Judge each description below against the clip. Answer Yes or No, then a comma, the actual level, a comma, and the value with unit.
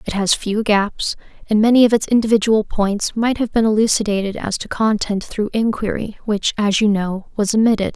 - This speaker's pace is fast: No, average, 190 wpm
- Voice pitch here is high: Yes, high, 210 Hz